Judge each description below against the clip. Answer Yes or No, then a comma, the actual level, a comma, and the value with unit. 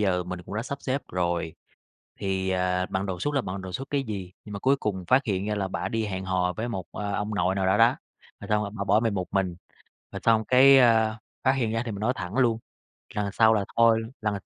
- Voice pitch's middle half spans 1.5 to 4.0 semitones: Yes, average, 3.3 semitones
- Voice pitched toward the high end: No, low, 105 Hz